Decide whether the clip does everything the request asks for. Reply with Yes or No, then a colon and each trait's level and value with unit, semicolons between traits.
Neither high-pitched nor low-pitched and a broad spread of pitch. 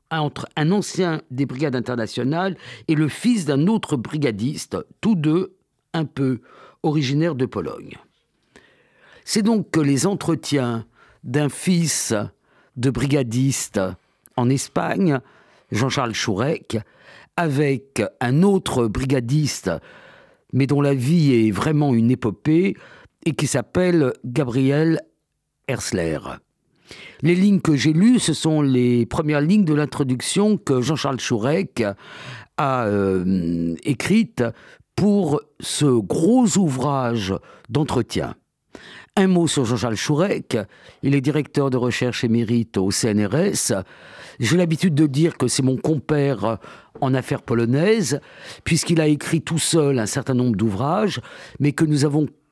No: medium, 145 Hz; average, 4.8 semitones